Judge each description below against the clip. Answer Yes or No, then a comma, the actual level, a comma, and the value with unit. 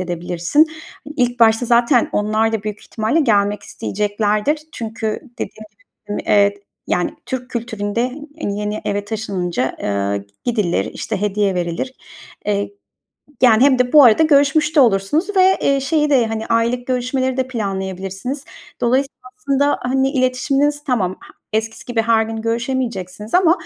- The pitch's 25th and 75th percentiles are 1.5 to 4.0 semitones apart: No, average, 4.4 semitones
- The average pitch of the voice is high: Yes, high, 230 Hz